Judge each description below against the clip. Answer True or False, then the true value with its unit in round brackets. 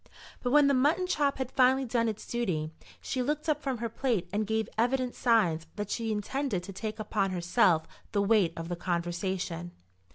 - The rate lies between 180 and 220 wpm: True (190 wpm)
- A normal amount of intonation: False (5.8 semitones)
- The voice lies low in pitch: False (220 Hz)